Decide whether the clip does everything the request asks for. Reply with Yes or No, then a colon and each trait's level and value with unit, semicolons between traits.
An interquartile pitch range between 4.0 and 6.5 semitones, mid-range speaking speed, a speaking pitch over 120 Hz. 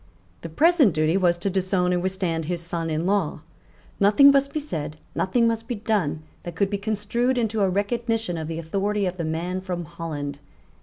Yes: average, 4.5 semitones; average, 195 wpm; medium, 185 Hz